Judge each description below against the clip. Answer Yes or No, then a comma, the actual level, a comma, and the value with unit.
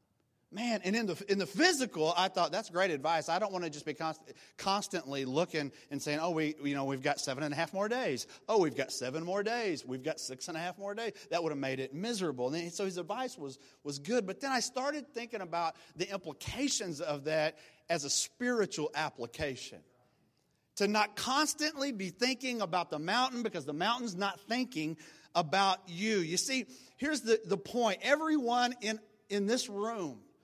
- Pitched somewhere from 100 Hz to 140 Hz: No, medium, 185 Hz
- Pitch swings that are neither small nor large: No, wide, 6.7 semitones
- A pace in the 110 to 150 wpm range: No, fast, 205 wpm